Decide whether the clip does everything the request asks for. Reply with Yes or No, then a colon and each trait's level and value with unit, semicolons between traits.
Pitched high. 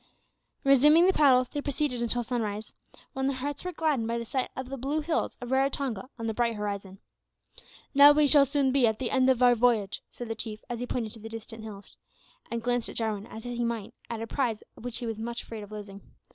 Yes: high, 240 Hz